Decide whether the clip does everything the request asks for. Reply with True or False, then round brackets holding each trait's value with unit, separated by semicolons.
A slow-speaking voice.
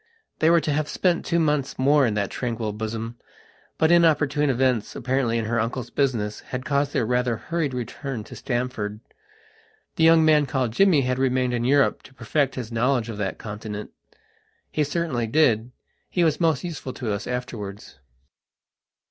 False (170 wpm)